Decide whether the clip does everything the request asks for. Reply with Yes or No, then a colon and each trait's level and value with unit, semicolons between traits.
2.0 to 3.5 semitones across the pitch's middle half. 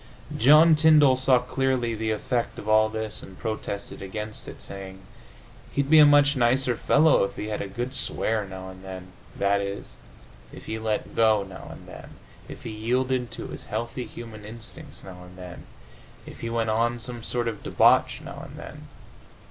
No: average, 4.0 semitones